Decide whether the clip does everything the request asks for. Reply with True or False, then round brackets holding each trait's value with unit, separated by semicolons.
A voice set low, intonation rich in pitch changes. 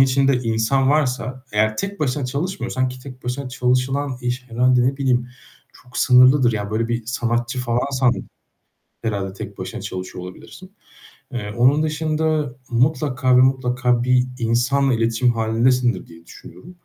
False (125 Hz; 2.4 semitones)